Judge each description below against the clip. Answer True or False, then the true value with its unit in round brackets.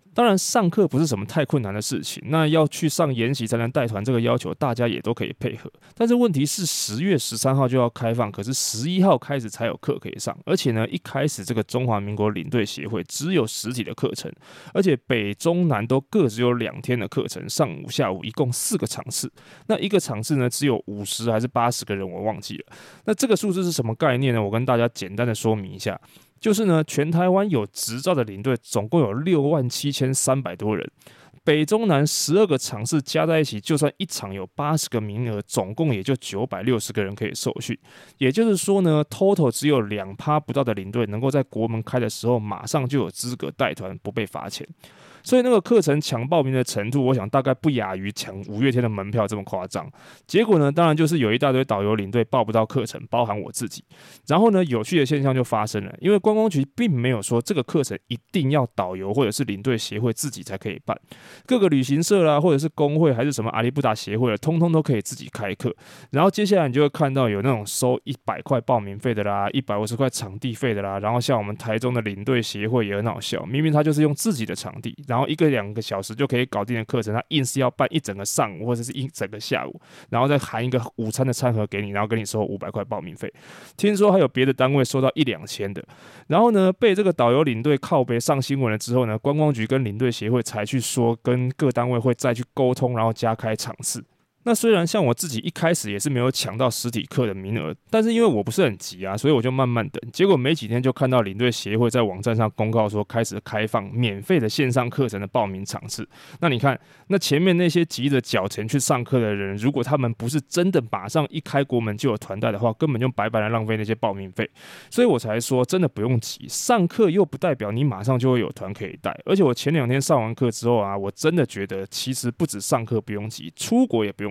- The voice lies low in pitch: True (125 Hz)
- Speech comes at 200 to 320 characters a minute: False (355 characters per minute)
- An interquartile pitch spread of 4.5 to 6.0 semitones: True (5.2 semitones)